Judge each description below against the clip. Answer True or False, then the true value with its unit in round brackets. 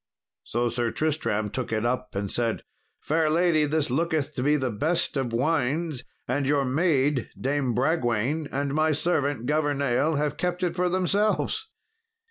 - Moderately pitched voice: True (145 Hz)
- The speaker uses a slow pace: False (155 wpm)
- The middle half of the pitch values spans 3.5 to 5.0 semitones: True (4.1 semitones)